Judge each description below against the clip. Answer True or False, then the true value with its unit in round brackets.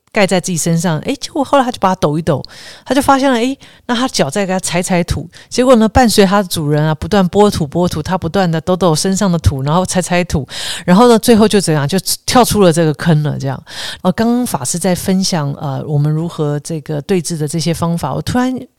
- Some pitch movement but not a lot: True (4.3 semitones)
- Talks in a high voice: False (180 Hz)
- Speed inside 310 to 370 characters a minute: True (345 characters per minute)